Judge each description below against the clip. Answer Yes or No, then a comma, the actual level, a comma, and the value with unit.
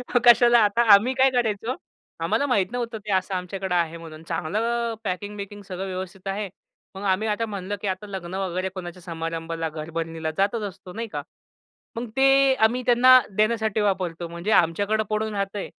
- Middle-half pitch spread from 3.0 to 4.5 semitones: Yes, average, 3.9 semitones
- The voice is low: No, high, 200 Hz